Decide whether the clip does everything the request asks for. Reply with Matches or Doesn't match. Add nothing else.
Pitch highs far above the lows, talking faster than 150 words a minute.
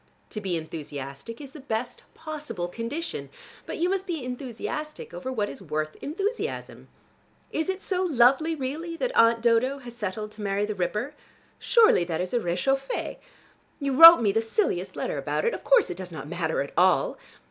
Matches